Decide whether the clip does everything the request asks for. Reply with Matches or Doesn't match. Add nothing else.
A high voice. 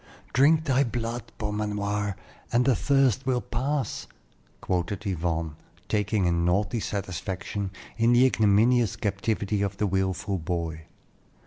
Doesn't match